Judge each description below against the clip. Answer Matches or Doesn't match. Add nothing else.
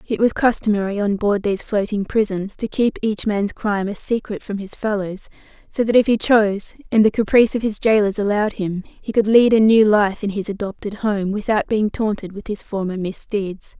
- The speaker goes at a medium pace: Doesn't match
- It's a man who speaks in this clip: Doesn't match